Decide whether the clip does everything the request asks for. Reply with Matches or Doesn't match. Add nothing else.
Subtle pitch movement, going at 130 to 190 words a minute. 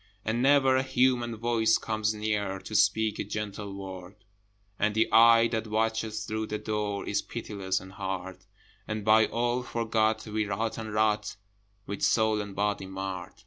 Matches